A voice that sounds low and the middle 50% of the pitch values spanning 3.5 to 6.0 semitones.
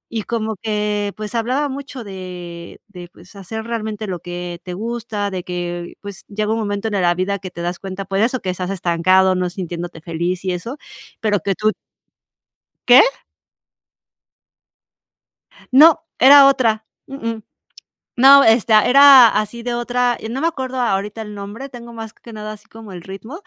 No: high, 210 Hz; average, 4.2 semitones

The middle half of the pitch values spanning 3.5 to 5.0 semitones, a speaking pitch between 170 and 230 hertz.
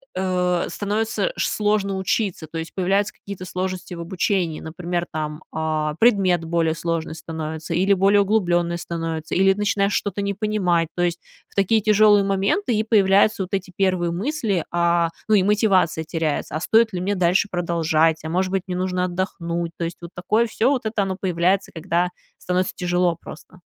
No: average, 2.8 semitones; medium, 185 Hz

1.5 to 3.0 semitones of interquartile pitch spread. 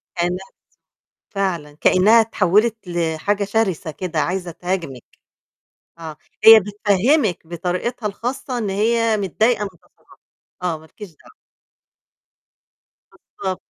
No: average, 4.2 semitones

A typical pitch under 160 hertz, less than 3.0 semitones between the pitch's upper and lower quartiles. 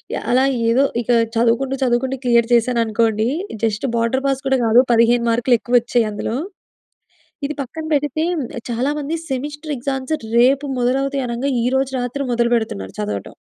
No: high, 245 Hz; narrow, 2.6 semitones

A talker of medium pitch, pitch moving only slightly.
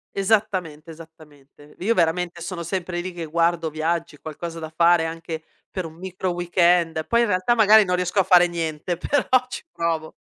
Yes: medium, 170 Hz; narrow, 2.1 semitones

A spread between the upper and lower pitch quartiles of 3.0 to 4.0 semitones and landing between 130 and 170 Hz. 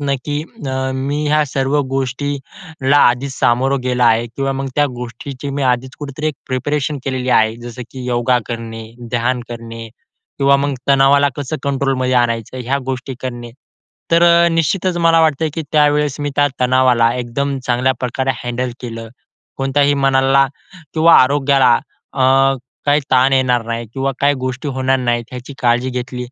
No: narrow, 2.4 semitones; low, 135 Hz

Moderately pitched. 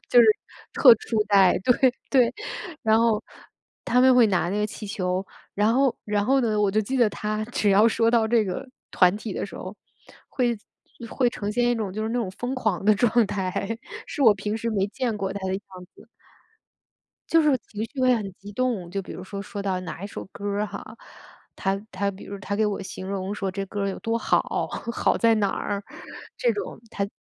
No: high, 210 Hz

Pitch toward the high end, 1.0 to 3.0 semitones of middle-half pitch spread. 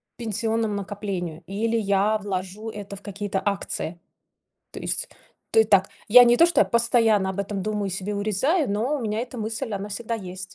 Yes: high, 210 Hz; narrow, 2.5 semitones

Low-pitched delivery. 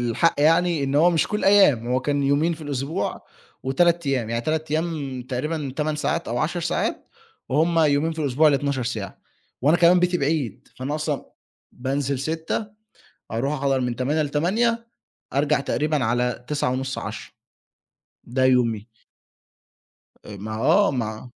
No: medium, 145 Hz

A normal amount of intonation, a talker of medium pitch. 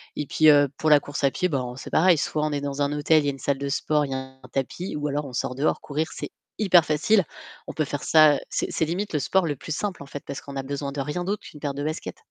No: narrow, 2.1 semitones; medium, 145 Hz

